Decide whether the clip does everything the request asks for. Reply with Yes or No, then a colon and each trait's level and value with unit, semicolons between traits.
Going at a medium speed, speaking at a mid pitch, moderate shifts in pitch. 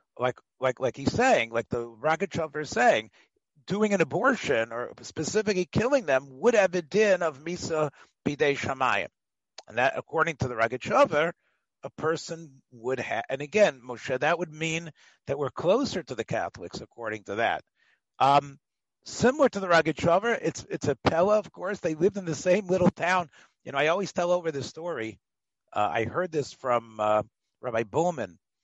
No: average, 175 wpm; medium, 155 Hz; wide, 6.0 semitones